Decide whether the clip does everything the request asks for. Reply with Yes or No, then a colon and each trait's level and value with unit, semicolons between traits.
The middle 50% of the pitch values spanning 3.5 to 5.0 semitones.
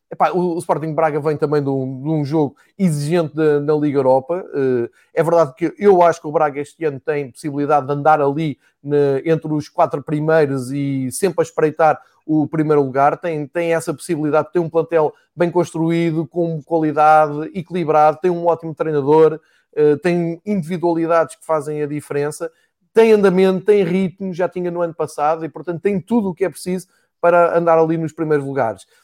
No: narrow, 2.5 semitones